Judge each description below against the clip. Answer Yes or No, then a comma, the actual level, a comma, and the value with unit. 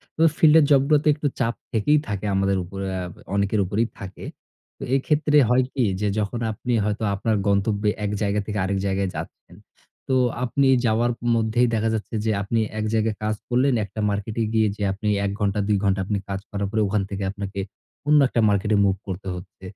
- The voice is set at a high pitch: No, low, 105 Hz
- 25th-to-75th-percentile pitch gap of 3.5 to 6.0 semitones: No, average, 3.1 semitones